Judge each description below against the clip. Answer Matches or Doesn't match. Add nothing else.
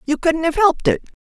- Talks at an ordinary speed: Doesn't match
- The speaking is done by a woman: Matches